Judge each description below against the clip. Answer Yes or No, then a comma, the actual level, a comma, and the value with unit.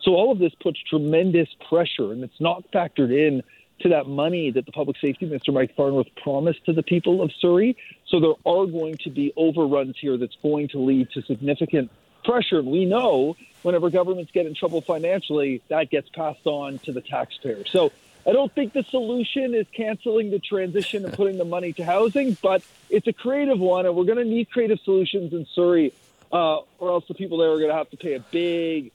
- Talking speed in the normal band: No, fast, 215 wpm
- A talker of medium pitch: Yes, medium, 170 Hz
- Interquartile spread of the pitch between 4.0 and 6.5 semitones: Yes, average, 4.3 semitones